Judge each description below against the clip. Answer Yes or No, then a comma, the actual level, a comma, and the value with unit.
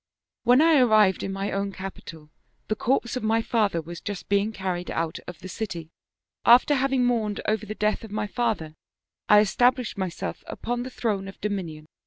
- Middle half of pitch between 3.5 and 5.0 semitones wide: Yes, average, 4.0 semitones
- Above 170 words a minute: Yes, average, 190 wpm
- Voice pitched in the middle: No, high, 210 Hz